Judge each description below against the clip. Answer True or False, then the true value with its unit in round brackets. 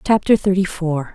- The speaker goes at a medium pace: True (155 wpm)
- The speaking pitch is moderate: True (180 Hz)